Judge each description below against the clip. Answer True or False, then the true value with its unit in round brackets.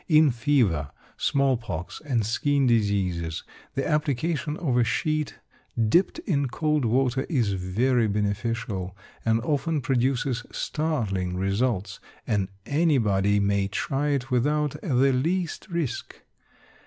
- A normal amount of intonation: False (6.2 semitones)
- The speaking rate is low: True (115 wpm)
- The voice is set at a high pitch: False (125 Hz)